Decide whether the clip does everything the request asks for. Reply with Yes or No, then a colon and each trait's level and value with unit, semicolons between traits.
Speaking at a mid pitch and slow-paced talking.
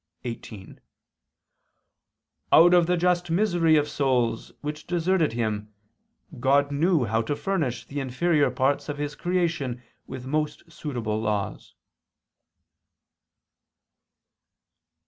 Yes: medium, 145 Hz; slow, 105 wpm